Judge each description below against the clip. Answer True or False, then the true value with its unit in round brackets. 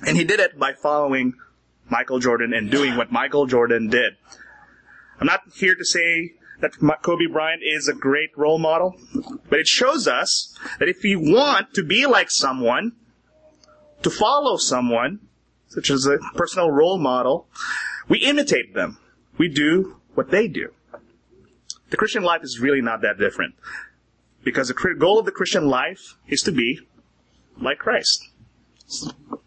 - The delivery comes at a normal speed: True (155 wpm)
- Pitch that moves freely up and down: True (5.9 semitones)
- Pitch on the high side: False (155 Hz)